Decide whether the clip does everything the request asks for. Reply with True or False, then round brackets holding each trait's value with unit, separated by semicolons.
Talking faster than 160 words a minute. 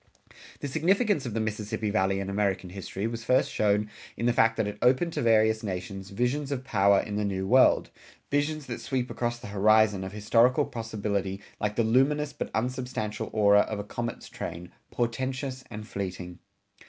True (180 wpm)